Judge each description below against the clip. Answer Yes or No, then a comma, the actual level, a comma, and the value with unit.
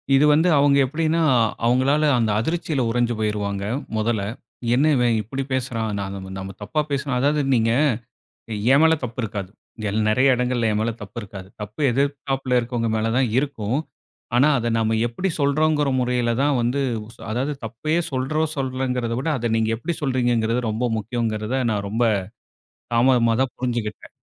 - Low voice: Yes, low, 125 Hz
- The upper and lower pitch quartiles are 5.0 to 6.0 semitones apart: No, average, 3.7 semitones